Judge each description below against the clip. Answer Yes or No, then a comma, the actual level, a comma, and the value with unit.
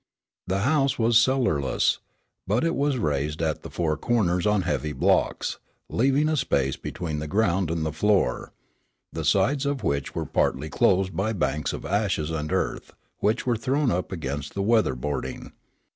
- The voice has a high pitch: No, very low, 95 Hz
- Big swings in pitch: Yes, wide, 7.4 semitones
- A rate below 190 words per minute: Yes, average, 170 wpm